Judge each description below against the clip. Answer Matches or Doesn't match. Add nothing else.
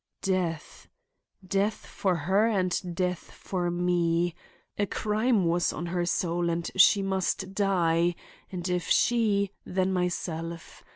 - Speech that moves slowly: Matches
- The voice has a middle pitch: Matches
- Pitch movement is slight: Matches